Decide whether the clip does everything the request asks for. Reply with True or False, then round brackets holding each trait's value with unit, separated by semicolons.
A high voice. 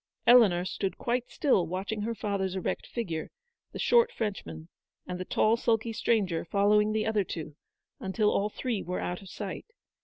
True (205 Hz)